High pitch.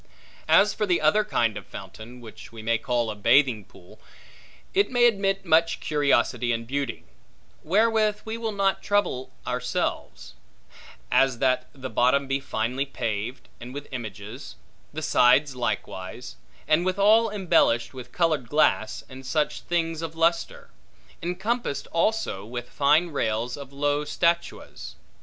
No: medium, 140 Hz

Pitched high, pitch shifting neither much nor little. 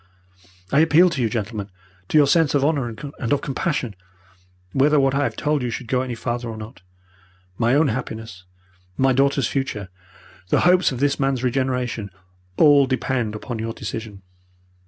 No: low, 130 Hz; average, 3.8 semitones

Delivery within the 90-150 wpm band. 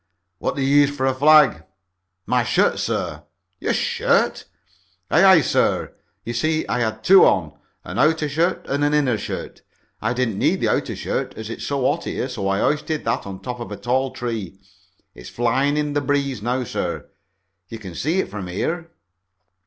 No: average, 190 wpm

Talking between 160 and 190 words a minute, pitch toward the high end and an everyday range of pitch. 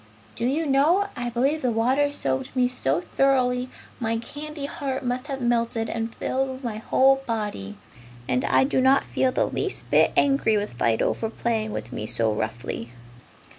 Yes: average, 170 wpm; high, 245 Hz; average, 3.8 semitones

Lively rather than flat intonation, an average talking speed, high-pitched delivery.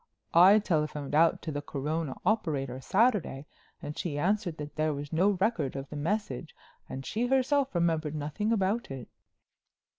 No: wide, 6.2 semitones; average, 155 wpm; medium, 160 Hz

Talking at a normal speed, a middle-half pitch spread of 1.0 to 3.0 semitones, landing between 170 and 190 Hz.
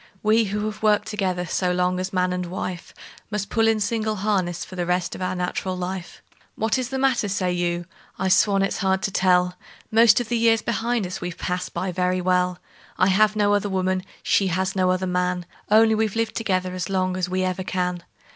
No: fast, 215 wpm; average, 2.7 semitones; medium, 185 Hz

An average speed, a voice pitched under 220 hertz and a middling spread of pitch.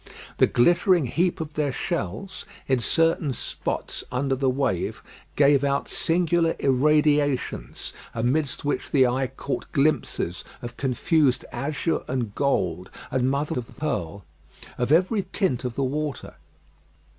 No: slow, 130 wpm; medium, 140 Hz; average, 3.7 semitones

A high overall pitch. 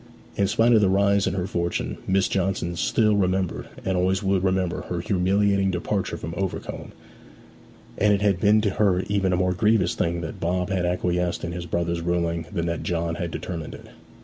No: very low, 90 Hz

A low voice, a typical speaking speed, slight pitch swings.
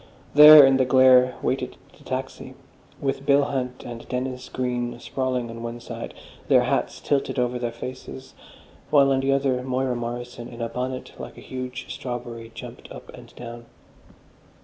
Yes: low, 125 Hz; average, 165 wpm; narrow, 1.6 semitones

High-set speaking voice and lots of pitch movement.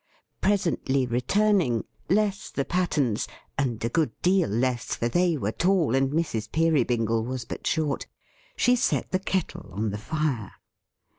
No: medium, 140 Hz; wide, 7.3 semitones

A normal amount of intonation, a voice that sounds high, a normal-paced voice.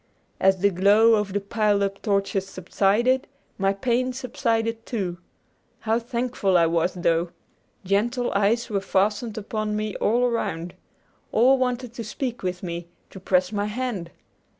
Yes: average, 3.5 semitones; high, 210 Hz; average, 150 wpm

